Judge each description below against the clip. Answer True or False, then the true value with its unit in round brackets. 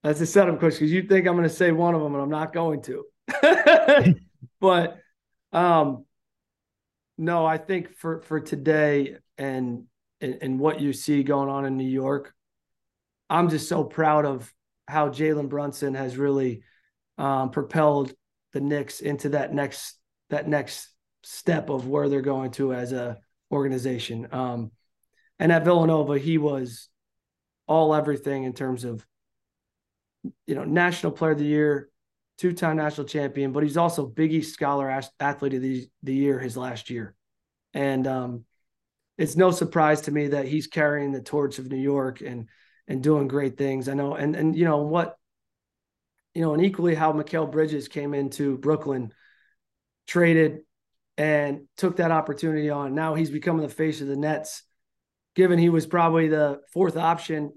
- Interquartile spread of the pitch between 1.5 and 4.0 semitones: True (2.8 semitones)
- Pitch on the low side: False (145 Hz)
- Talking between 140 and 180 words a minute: True (165 wpm)